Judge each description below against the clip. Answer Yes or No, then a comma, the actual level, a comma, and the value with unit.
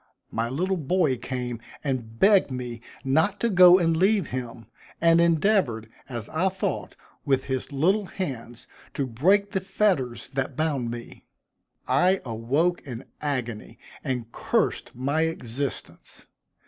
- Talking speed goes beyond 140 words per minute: No, slow, 135 wpm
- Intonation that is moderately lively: No, wide, 6.7 semitones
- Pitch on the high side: No, medium, 140 Hz